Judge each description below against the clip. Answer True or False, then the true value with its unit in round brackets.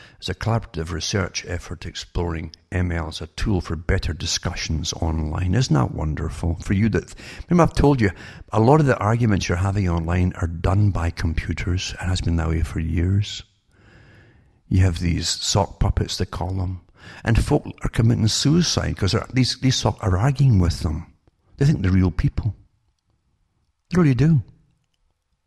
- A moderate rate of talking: True (175 wpm)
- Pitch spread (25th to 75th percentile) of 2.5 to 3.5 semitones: False (4.6 semitones)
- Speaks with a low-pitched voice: True (95 Hz)